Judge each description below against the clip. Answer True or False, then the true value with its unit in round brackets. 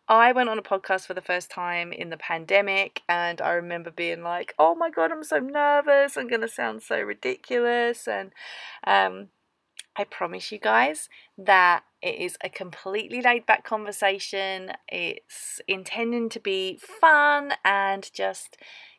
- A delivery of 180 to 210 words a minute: False (160 wpm)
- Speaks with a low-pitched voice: False (200 Hz)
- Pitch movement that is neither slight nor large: False (6.2 semitones)